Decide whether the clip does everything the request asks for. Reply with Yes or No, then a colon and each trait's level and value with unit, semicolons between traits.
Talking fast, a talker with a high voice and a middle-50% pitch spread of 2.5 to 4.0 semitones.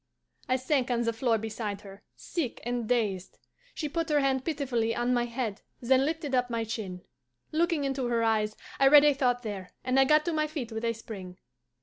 Yes: fast, 210 wpm; high, 245 Hz; average, 3.6 semitones